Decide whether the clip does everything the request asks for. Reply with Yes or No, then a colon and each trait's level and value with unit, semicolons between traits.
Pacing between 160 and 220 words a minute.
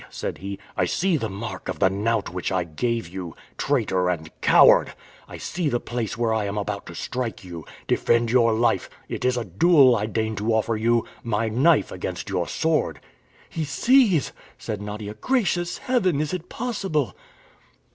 Yes: average, 175 wpm